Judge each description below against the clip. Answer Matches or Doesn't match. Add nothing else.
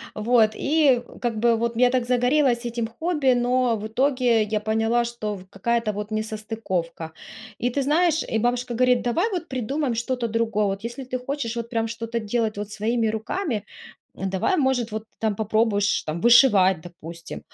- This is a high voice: Matches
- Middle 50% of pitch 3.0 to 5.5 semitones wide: Doesn't match